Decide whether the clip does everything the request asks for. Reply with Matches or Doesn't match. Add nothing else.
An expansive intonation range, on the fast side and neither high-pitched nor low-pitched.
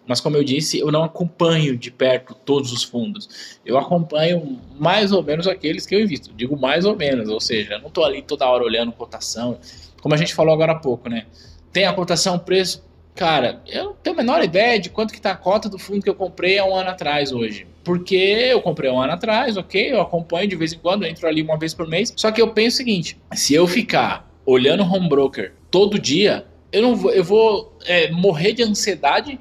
Matches